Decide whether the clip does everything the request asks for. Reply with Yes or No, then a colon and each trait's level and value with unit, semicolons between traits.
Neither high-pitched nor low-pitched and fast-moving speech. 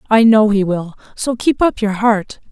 No: high, 215 Hz; fast, 215 wpm